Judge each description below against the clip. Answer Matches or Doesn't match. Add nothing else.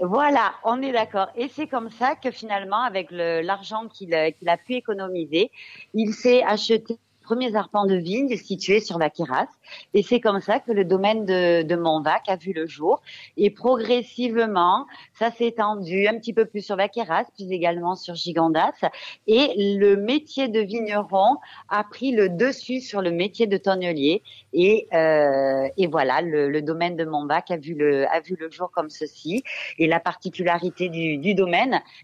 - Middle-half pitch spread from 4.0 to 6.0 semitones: Matches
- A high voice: Matches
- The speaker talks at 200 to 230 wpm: Doesn't match